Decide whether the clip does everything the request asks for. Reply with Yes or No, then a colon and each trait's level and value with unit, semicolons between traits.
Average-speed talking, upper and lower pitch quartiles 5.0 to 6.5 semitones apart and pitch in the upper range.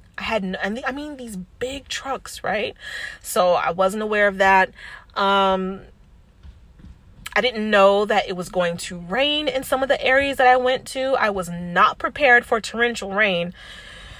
Yes: average, 175 wpm; wide, 5.5 semitones; high, 215 Hz